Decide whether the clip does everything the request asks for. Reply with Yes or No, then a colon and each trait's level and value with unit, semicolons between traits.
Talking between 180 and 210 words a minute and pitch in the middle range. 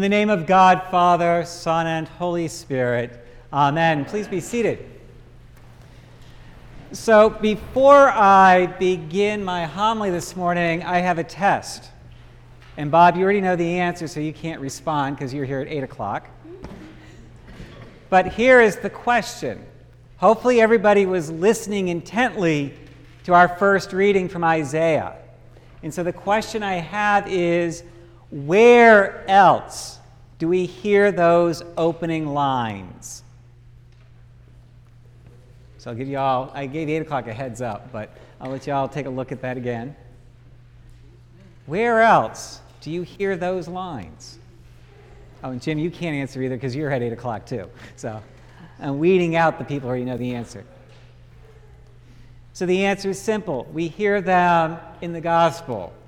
No: average, 150 wpm; medium, 160 Hz